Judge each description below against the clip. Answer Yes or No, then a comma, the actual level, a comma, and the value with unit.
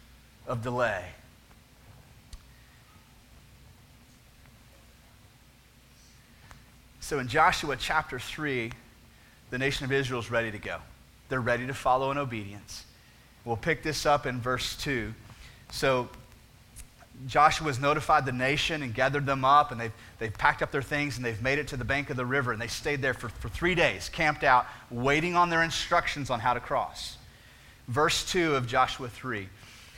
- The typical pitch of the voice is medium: No, low, 125 Hz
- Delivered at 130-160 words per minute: Yes, average, 155 wpm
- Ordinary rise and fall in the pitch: Yes, average, 3.4 semitones